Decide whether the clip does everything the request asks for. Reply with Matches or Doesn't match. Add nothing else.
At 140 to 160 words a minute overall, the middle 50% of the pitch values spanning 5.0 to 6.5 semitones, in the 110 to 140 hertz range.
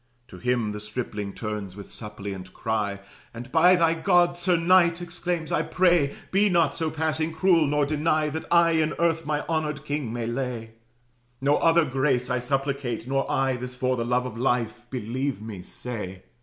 Doesn't match